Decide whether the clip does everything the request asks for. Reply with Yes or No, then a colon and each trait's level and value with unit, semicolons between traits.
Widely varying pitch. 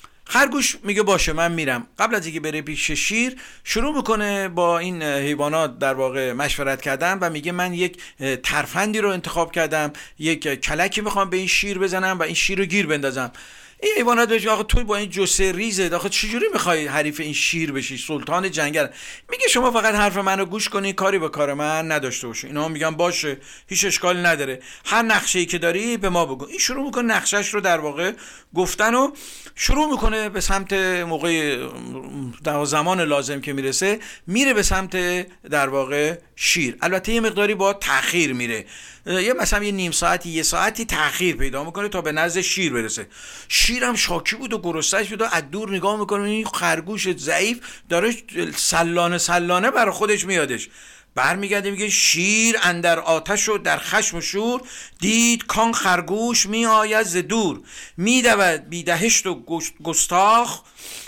No: average, 4.9 semitones